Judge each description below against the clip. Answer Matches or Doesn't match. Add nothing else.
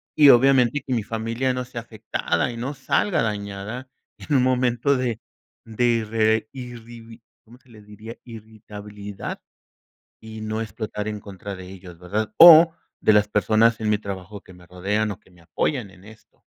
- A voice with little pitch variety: Doesn't match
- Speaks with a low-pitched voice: Matches